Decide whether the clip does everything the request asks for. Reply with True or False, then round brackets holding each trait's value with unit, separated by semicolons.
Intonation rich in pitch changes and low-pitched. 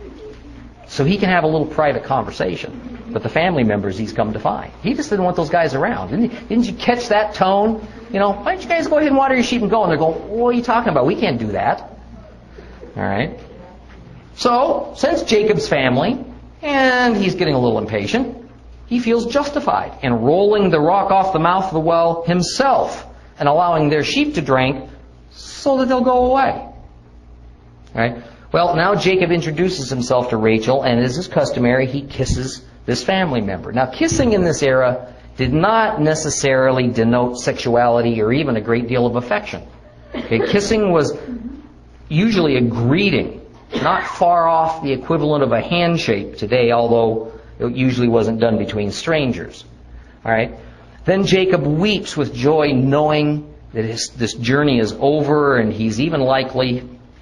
False (8.9 semitones; 150 Hz)